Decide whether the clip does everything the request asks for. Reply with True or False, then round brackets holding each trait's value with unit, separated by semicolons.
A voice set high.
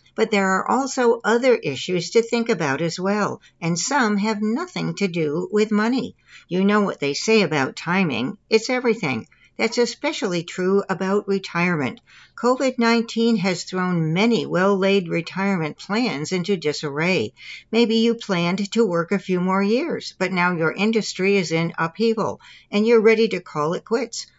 True (200 Hz)